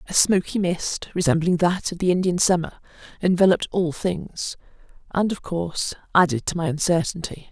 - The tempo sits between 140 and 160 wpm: Yes, average, 150 wpm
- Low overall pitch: No, medium, 175 Hz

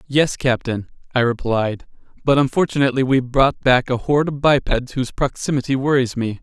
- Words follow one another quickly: No, average, 160 wpm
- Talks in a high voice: No, low, 130 Hz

